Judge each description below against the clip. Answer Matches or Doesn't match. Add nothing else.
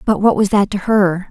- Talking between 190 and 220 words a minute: Doesn't match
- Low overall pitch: Doesn't match